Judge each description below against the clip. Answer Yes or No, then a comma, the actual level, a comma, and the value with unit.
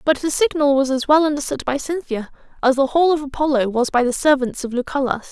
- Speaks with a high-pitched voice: Yes, very high, 280 Hz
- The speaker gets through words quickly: Yes, fast, 225 wpm